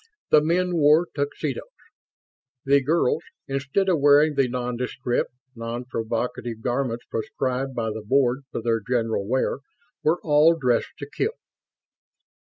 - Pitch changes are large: No, average, 3.6 semitones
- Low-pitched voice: Yes, low, 130 Hz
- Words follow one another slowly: Yes, slow, 130 wpm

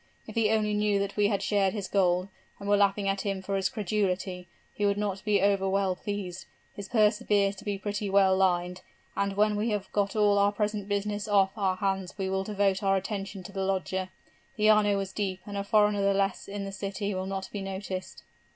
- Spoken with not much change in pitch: Yes, narrow, 1.3 semitones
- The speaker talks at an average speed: No, fast, 225 wpm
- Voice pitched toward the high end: Yes, high, 200 Hz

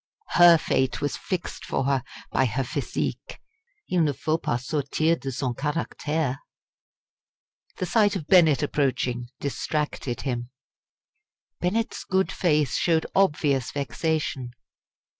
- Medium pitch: Yes, medium, 150 Hz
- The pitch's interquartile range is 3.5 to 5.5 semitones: Yes, average, 3.9 semitones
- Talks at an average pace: No, slow, 120 wpm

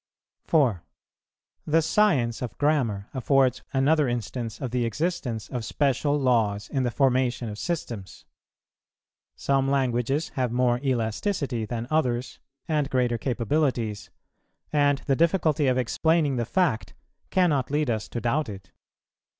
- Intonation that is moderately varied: Yes, average, 3.8 semitones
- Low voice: Yes, low, 130 Hz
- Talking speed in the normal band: No, slow, 130 wpm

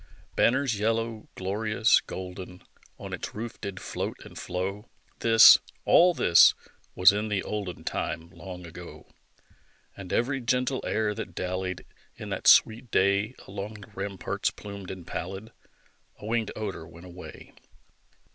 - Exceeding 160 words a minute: No, slow, 135 wpm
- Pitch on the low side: Yes, low, 100 Hz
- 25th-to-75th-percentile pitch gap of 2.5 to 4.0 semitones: Yes, average, 3.3 semitones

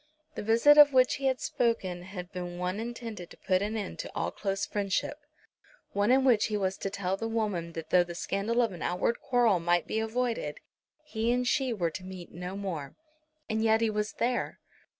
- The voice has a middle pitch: No, high, 210 Hz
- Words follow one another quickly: Yes, fast, 210 wpm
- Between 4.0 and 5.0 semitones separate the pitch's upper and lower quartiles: Yes, average, 4.3 semitones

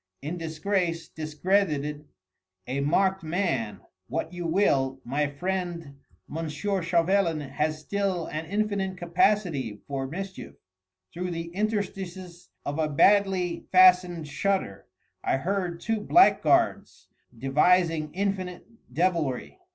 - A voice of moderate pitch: Yes, medium, 170 Hz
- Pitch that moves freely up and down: No, average, 4.0 semitones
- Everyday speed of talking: No, slow, 105 wpm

